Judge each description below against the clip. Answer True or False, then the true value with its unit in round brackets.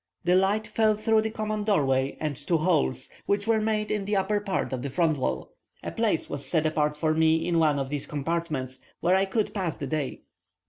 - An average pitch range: False (5.8 semitones)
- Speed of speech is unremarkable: False (225 wpm)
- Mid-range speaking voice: True (170 Hz)